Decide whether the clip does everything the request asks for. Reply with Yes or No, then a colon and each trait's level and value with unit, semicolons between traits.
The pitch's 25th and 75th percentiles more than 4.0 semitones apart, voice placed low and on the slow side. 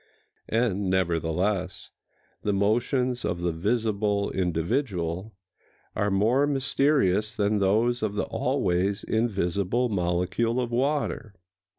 Yes: average, 4.5 semitones; low, 105 Hz; slow, 100 wpm